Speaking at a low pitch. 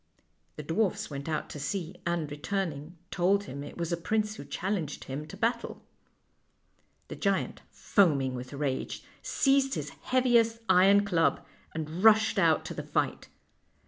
No: medium, 175 Hz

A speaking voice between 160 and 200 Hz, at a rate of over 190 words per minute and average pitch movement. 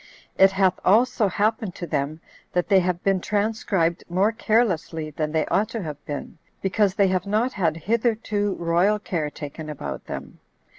No: high, 190 Hz; average, 165 wpm; average, 4.4 semitones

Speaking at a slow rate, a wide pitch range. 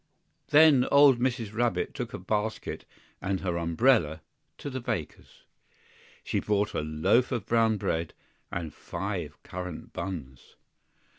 Yes: slow, 130 wpm; wide, 6.2 semitones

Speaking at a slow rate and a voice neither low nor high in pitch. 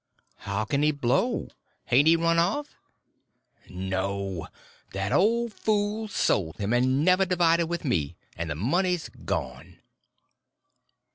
Yes: slow, 125 wpm; medium, 150 Hz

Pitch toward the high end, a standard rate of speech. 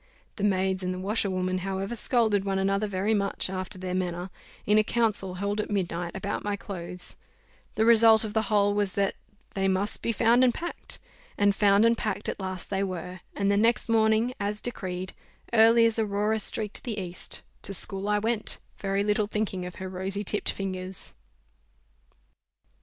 Yes: high, 200 Hz; average, 180 wpm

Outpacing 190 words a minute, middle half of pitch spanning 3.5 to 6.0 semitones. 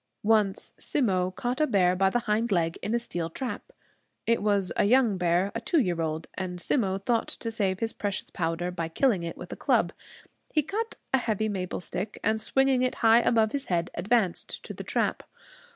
Yes: average, 200 wpm; average, 4.6 semitones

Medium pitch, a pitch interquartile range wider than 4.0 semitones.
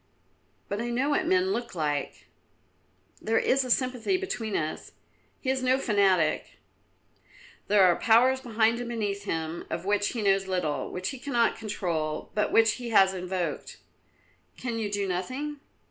No: high, 220 Hz; average, 5.1 semitones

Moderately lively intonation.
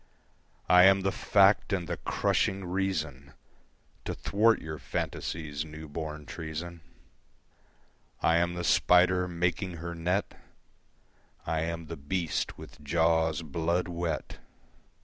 No: narrow, 2.3 semitones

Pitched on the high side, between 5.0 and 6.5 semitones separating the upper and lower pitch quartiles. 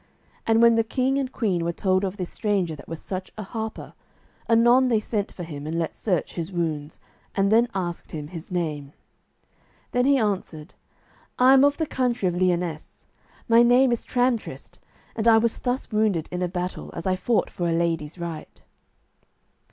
Yes: high, 195 Hz; wide, 5.5 semitones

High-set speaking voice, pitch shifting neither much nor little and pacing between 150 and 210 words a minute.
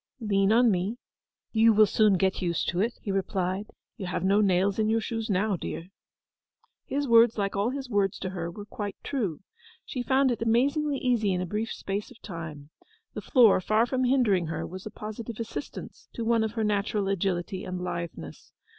Yes: high, 210 Hz; average, 3.5 semitones; average, 195 wpm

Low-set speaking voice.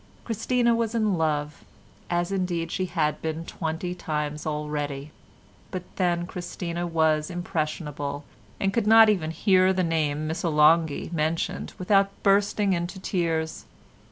No: medium, 170 Hz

